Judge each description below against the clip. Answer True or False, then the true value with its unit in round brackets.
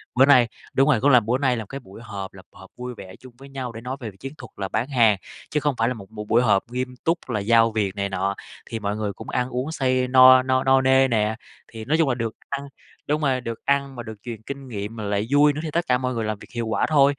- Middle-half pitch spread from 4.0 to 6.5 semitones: False (3.5 semitones)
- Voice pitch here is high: False (125 Hz)